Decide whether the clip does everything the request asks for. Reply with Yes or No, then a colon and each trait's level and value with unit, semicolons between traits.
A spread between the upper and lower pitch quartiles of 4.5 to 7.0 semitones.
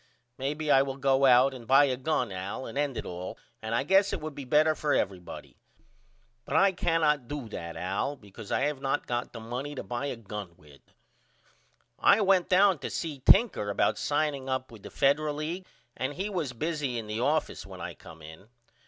Yes: average, 5.1 semitones